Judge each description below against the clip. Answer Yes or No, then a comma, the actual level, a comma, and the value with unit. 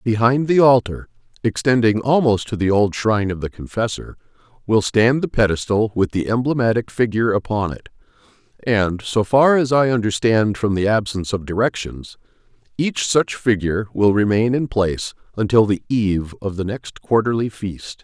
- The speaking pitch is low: Yes, low, 110 Hz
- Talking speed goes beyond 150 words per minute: No, average, 145 wpm